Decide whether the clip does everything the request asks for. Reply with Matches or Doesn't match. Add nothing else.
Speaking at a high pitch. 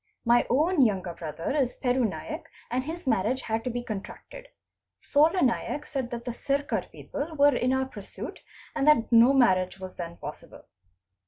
Matches